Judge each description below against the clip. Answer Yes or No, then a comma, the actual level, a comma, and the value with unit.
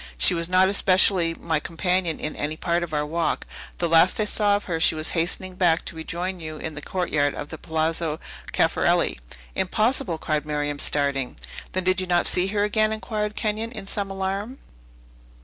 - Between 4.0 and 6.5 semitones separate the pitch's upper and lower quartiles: No, average, 3.6 semitones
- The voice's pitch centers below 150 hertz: No, medium, 175 Hz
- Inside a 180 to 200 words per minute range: Yes, average, 185 wpm